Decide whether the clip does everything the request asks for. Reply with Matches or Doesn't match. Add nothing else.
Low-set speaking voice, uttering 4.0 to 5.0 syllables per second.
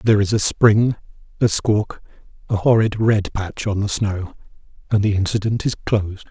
Matches